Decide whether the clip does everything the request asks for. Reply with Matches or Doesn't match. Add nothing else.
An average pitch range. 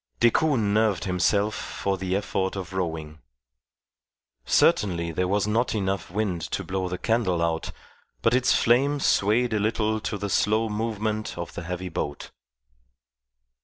Matches